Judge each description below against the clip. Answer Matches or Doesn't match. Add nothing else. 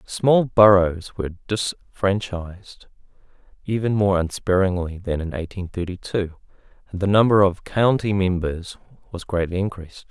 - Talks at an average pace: Doesn't match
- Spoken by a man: Matches